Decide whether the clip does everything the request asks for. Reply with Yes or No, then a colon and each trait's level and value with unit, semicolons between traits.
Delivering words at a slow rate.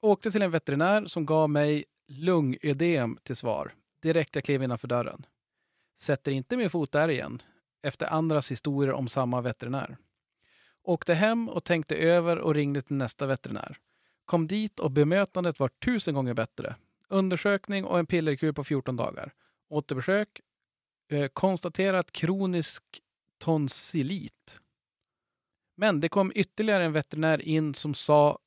No: average, 135 wpm